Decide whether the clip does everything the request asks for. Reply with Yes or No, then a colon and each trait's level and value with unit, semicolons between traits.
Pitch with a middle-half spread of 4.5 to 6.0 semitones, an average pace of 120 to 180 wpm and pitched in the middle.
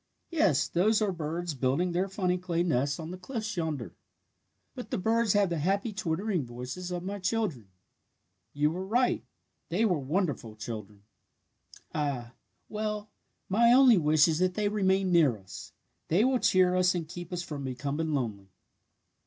Yes: average, 5.3 semitones; average, 165 wpm; medium, 175 Hz